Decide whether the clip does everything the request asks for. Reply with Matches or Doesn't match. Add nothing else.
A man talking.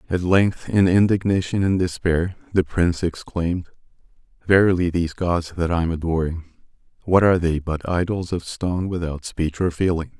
Matches